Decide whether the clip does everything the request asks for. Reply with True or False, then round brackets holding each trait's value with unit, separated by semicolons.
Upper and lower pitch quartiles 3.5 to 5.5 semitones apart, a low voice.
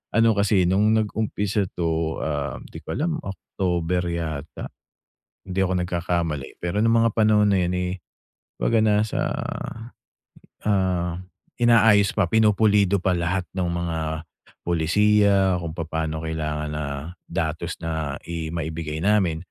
True (4.0 semitones; 90 Hz)